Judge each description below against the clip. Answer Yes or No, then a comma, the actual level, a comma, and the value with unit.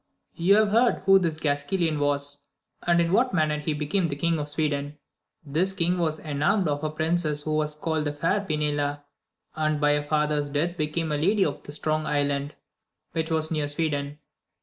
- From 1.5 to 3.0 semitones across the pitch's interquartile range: Yes, narrow, 2.5 semitones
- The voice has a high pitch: No, medium, 155 Hz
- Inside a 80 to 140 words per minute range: No, average, 180 wpm